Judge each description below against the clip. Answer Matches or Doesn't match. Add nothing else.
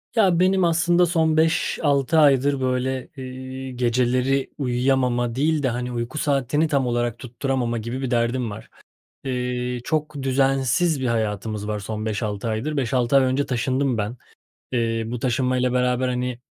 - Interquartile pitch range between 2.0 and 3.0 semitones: Matches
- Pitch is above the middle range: Doesn't match